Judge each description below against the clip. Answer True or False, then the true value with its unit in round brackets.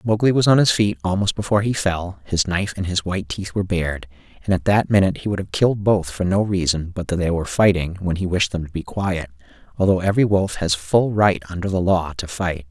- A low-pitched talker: True (90 Hz)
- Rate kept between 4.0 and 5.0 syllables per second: False (6.1 syllables/s)